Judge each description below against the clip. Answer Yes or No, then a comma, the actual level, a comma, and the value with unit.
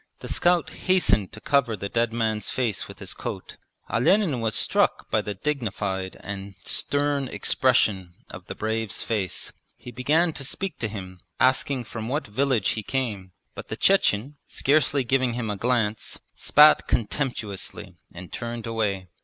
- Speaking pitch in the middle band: No, low, 115 Hz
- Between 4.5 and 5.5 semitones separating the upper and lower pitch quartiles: Yes, average, 4.8 semitones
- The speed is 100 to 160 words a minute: Yes, average, 155 wpm